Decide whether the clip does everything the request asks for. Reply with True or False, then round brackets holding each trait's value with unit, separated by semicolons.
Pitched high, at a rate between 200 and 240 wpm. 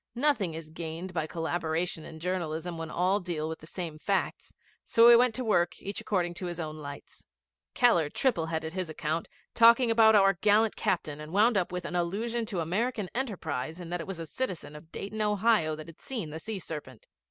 False (175 Hz; 205 wpm)